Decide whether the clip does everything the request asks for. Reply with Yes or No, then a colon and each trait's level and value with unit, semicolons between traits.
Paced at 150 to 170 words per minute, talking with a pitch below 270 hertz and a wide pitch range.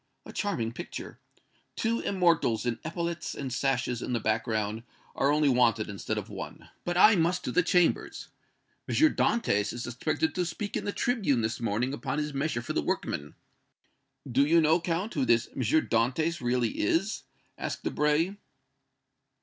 Yes: average, 165 wpm; medium, 140 Hz; wide, 6.3 semitones